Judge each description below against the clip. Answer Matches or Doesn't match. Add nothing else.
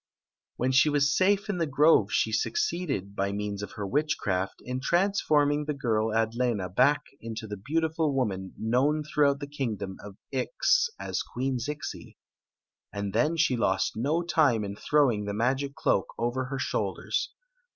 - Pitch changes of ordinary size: Doesn't match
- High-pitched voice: Doesn't match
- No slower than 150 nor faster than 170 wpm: Matches